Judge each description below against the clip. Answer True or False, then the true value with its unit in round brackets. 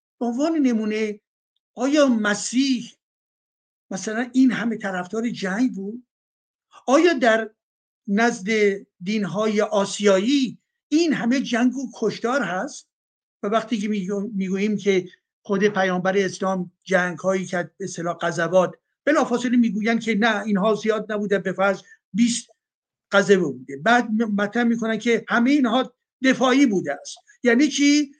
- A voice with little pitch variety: False (3.8 semitones)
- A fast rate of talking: False (130 wpm)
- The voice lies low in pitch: False (220 Hz)